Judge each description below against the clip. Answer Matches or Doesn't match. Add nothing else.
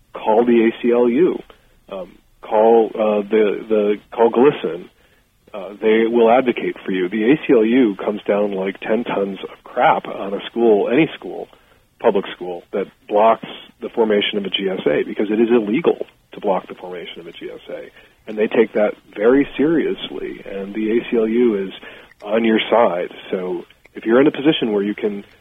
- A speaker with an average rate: Matches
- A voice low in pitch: Matches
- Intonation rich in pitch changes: Doesn't match